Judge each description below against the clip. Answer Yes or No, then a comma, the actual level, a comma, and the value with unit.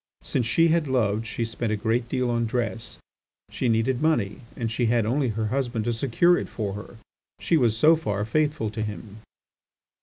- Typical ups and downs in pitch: Yes, average, 3.0 semitones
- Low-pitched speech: Yes, low, 115 Hz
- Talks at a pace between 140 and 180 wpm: No, average, 190 wpm